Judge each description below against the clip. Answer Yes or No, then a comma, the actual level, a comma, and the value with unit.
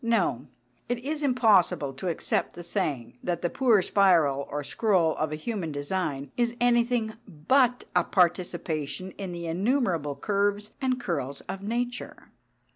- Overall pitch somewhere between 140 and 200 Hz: Yes, medium, 185 Hz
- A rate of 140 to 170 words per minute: Yes, average, 145 wpm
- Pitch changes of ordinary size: No, wide, 7.1 semitones